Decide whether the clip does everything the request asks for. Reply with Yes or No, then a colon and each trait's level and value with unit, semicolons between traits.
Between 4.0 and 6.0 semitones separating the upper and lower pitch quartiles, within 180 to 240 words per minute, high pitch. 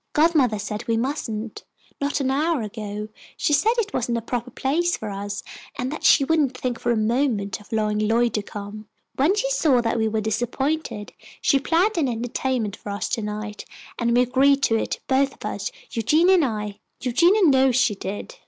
Yes: average, 4.9 semitones; average, 195 wpm; high, 245 Hz